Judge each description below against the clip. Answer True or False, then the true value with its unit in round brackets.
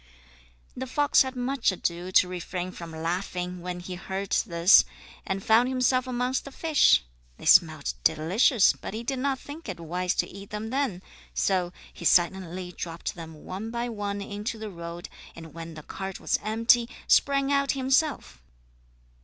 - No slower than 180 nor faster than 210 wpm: False (165 wpm)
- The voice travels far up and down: True (6.0 semitones)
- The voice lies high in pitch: True (195 Hz)